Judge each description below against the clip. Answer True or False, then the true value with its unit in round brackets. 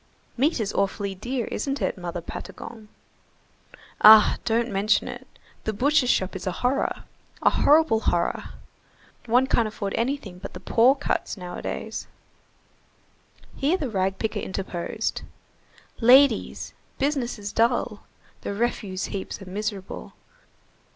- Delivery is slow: True (125 wpm)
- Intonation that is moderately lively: True (4.2 semitones)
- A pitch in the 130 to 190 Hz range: False (220 Hz)